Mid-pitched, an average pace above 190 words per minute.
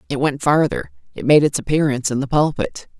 Yes: medium, 145 Hz; average, 200 wpm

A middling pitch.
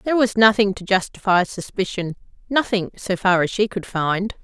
No: high, 200 Hz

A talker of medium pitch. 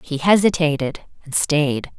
Yes: medium, 155 Hz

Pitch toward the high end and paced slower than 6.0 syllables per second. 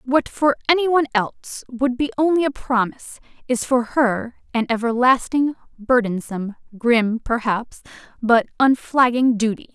Yes: high, 245 Hz; 4.7 syllables/s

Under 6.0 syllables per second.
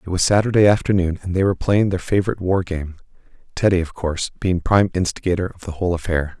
No: 6.9 syllables/s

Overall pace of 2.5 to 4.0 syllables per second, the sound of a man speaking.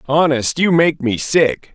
Yes: 3.8 syllables/s; male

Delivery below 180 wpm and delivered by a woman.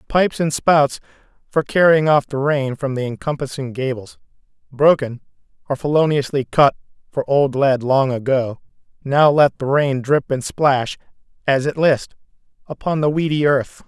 No: average, 150 wpm; male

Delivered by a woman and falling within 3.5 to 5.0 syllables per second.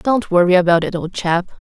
No: female; 5.3 syllables/s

